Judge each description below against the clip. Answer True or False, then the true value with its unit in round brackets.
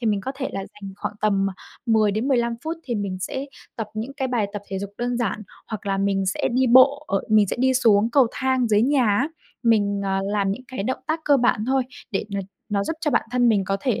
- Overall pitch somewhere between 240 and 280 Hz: False (225 Hz)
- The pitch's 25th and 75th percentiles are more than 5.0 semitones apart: False (4.4 semitones)